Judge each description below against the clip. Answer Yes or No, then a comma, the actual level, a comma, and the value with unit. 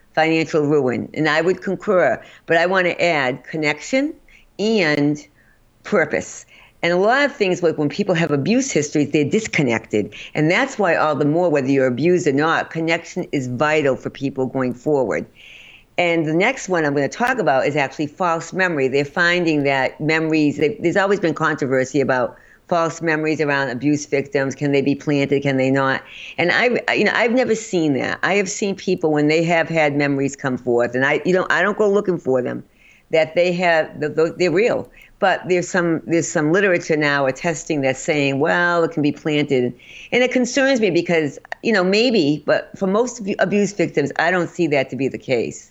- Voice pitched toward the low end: No, medium, 160 Hz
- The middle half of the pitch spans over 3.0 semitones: Yes, average, 3.9 semitones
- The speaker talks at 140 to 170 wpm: No, average, 195 wpm